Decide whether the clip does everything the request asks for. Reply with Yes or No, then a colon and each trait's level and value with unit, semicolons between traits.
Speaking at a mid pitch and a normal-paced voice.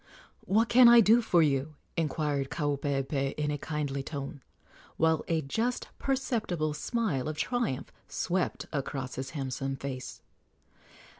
No: medium, 150 Hz; slow, 130 wpm